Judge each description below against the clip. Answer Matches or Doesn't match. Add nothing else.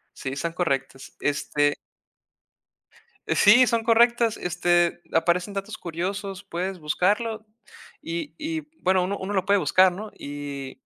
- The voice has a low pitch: Doesn't match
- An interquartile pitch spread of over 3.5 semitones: Matches